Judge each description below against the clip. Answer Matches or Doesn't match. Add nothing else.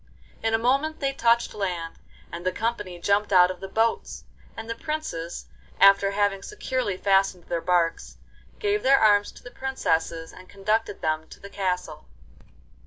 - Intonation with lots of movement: Doesn't match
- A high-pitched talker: Matches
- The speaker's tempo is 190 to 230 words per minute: Doesn't match